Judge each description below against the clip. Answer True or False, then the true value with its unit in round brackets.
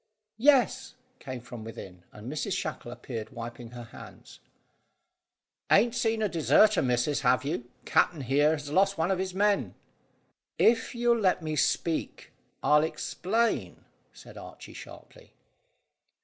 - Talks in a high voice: False (155 Hz)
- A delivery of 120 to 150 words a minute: True (135 wpm)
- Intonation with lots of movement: True (8.9 semitones)